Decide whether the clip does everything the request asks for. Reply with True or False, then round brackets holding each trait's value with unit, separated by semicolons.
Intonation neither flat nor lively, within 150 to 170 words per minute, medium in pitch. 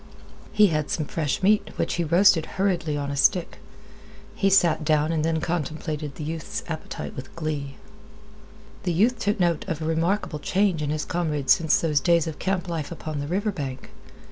False (3.5 semitones; 185 wpm; 165 Hz)